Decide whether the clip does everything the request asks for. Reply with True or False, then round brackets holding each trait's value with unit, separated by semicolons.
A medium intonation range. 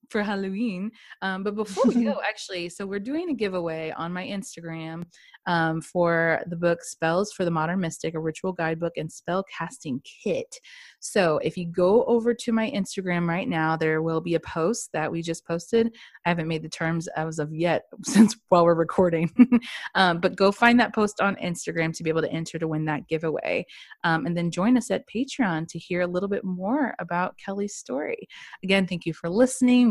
True (4.3 semitones)